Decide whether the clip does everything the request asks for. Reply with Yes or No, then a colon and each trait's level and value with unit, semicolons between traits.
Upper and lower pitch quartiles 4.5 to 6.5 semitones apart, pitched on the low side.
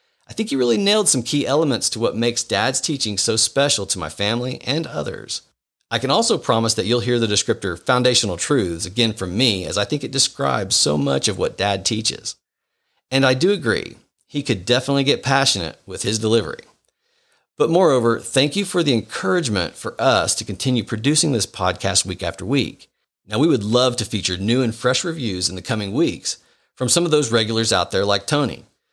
Yes: average, 4.8 semitones; low, 120 Hz